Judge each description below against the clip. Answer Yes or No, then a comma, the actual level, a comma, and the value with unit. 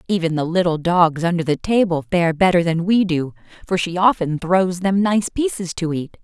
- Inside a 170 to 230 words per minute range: Yes, average, 200 wpm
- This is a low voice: No, medium, 175 Hz